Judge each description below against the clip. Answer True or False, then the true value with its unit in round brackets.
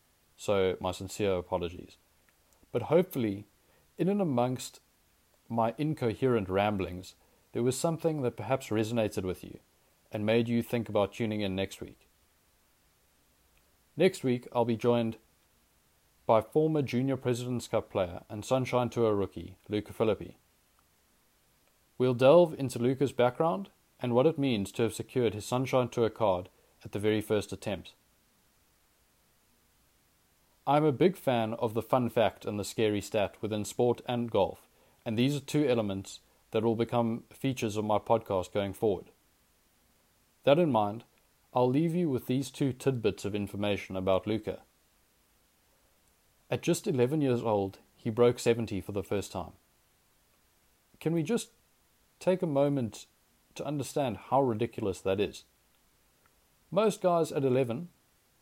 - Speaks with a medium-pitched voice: False (115 Hz)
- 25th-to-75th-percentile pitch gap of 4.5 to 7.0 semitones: True (5.0 semitones)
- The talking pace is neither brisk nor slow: True (145 wpm)